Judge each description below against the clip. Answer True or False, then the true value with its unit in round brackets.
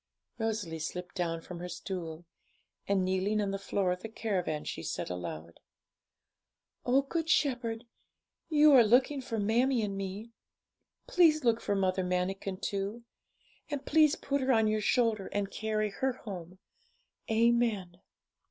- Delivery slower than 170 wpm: True (145 wpm)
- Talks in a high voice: True (210 Hz)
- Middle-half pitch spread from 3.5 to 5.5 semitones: True (4.7 semitones)